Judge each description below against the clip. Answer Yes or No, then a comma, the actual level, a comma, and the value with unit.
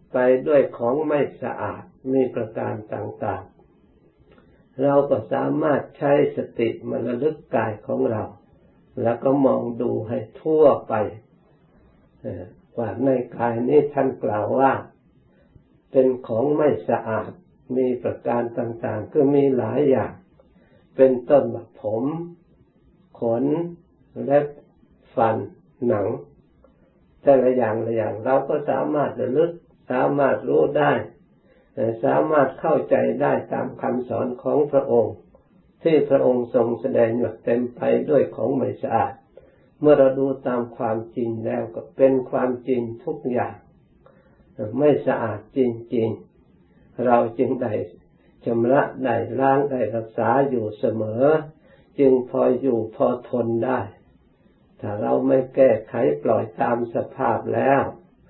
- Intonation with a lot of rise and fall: No, average, 2.8 semitones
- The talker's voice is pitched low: Yes, low, 130 Hz